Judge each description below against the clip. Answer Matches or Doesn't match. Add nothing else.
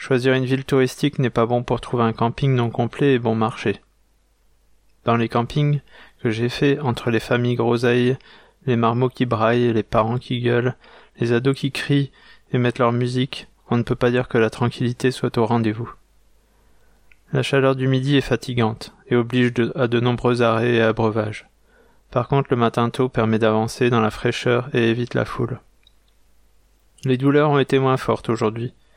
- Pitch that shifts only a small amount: Matches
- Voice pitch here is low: Matches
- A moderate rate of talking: Matches